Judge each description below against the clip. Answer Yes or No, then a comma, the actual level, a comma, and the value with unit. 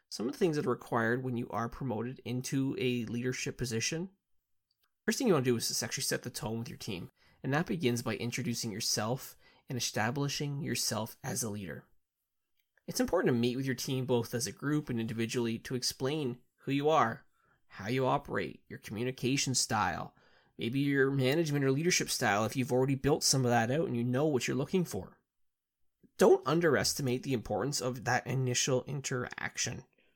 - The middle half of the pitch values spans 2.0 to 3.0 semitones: Yes, narrow, 2.6 semitones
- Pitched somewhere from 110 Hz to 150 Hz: Yes, low, 125 Hz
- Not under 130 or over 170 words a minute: No, average, 190 wpm